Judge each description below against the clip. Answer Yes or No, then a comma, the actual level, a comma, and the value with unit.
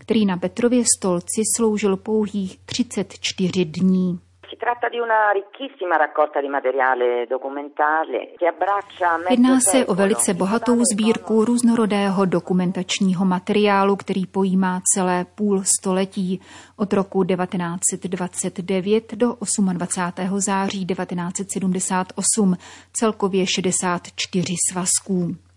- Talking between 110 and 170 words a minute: No, slow, 75 wpm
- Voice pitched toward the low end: No, high, 190 Hz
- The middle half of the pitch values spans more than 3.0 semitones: No, narrow, 2.6 semitones